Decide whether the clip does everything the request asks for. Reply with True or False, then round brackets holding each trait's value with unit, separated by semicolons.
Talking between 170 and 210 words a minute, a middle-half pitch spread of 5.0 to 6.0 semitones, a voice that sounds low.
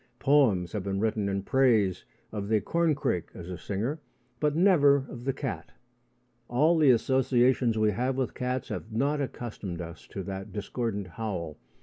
False (160 wpm; 5.3 semitones; 115 Hz)